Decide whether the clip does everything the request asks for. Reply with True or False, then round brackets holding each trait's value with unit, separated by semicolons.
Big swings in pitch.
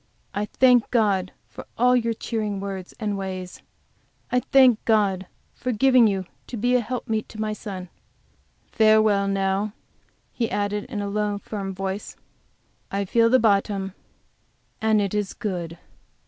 False (2.5 semitones)